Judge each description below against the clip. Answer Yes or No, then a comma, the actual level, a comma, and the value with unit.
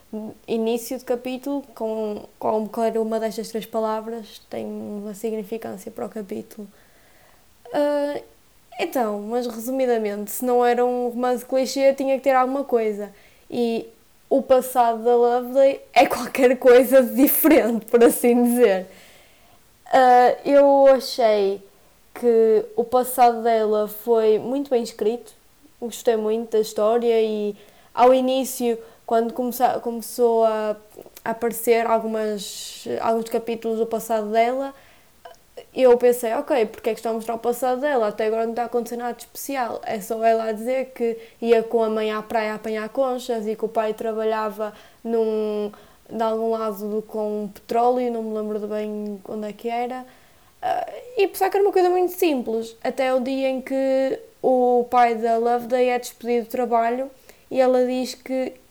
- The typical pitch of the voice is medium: No, high, 235 Hz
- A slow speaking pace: No, average, 155 wpm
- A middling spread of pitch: No, narrow, 2.3 semitones